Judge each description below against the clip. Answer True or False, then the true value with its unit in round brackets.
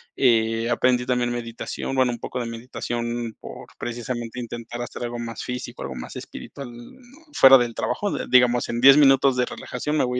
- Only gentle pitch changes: True (1.5 semitones)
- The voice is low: True (120 Hz)